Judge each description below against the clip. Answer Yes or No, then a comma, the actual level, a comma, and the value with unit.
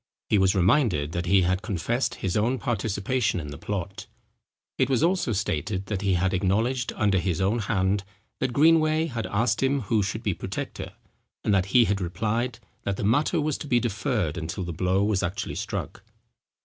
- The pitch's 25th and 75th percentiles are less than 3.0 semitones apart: No, average, 4.4 semitones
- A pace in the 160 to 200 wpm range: Yes, average, 190 wpm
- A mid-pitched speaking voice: No, low, 100 Hz